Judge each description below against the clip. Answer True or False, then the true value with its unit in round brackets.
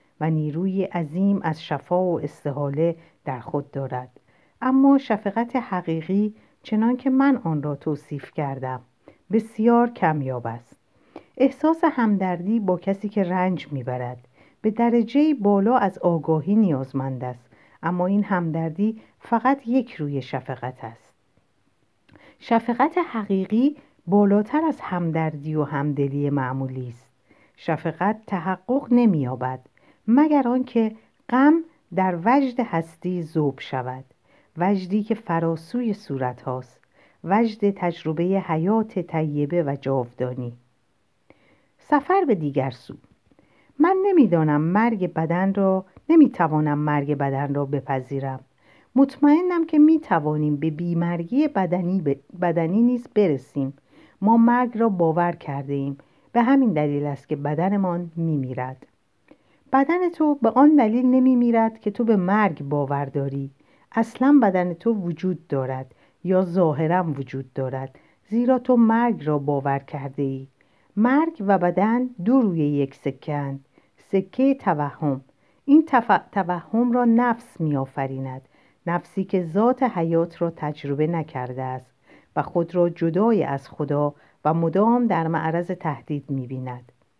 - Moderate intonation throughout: False (8.0 semitones)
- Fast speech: False (125 wpm)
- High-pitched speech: False (175 Hz)